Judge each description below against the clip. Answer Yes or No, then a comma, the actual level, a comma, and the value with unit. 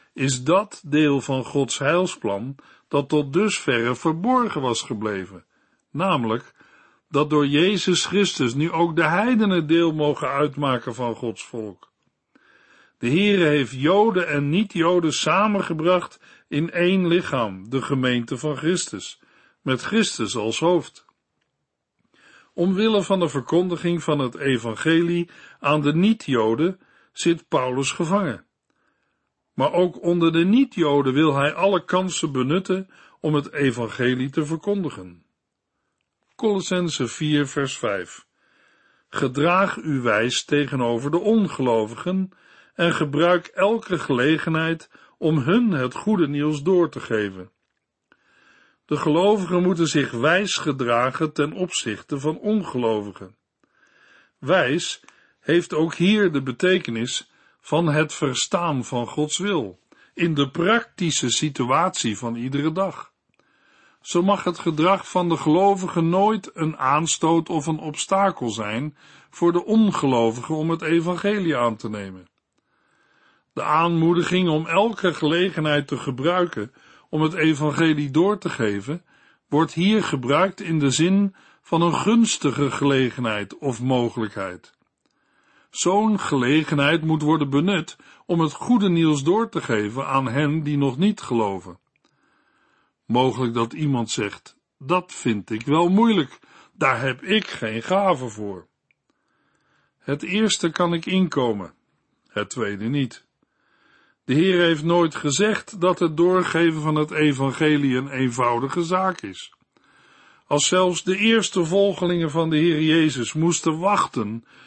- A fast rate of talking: No, slow, 125 wpm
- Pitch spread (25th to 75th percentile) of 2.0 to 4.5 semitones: No, average, 4.9 semitones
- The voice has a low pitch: No, medium, 155 Hz